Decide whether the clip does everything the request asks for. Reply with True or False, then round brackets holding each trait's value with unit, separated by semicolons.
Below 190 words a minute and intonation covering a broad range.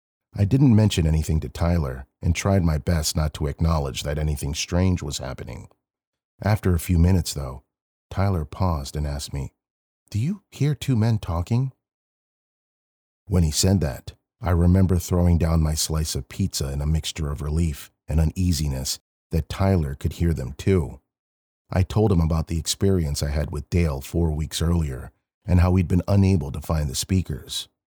False (175 wpm; 4.0 semitones)